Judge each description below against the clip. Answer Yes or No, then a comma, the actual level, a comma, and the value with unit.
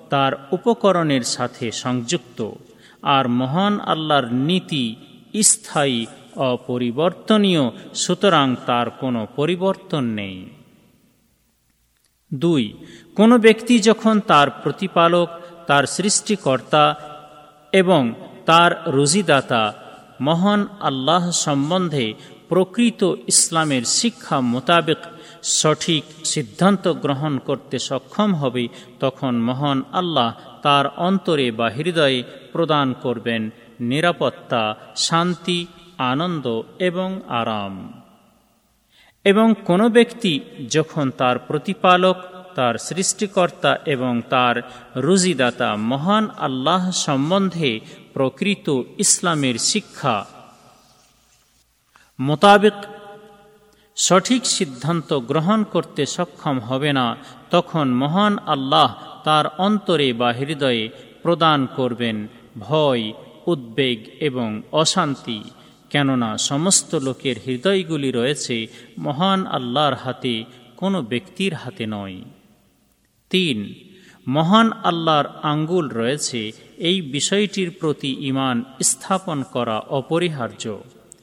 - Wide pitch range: Yes, wide, 6.4 semitones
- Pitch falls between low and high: Yes, medium, 150 Hz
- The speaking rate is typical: Yes, average, 85 wpm